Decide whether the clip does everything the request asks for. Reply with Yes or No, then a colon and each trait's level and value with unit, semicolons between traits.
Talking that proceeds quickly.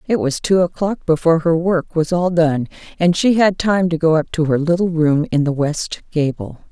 Yes: fast, 225 wpm